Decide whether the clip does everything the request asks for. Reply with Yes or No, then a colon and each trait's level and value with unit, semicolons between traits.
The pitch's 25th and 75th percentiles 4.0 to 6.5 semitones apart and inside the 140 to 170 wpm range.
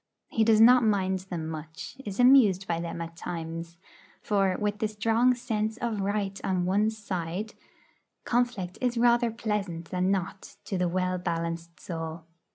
Yes: average, 4.4 semitones; average, 160 wpm